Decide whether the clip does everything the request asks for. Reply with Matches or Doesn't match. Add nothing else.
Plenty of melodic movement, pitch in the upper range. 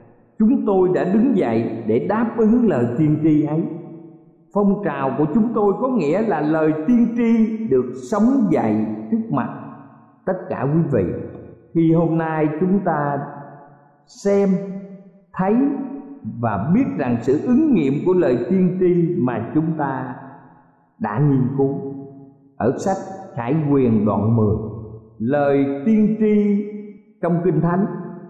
Doesn't match